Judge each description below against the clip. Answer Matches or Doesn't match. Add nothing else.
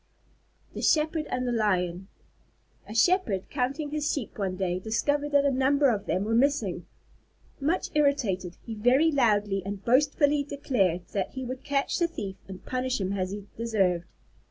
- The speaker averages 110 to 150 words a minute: Doesn't match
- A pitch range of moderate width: Doesn't match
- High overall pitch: Matches